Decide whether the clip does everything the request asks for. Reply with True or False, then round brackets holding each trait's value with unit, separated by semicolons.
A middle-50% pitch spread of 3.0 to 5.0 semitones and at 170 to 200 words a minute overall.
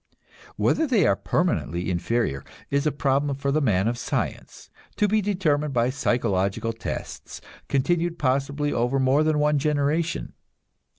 False (4.2 semitones; 140 wpm)